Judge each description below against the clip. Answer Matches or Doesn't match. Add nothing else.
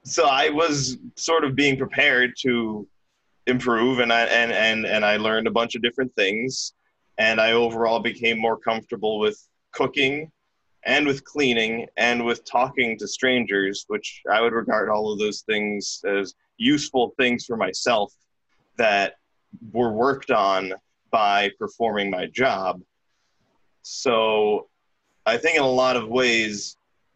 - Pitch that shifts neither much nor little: Matches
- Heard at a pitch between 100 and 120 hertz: Matches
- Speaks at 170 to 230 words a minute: Doesn't match